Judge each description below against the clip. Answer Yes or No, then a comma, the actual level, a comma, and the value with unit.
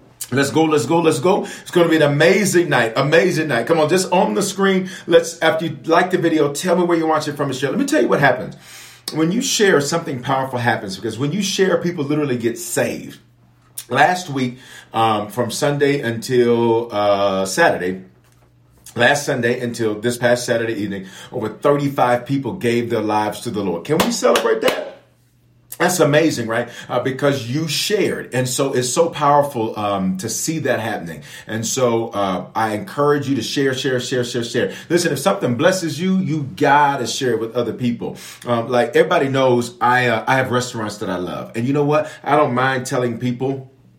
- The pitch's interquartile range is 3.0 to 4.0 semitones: No, average, 5.0 semitones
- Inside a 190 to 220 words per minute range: Yes, average, 200 wpm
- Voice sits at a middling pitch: No, low, 130 Hz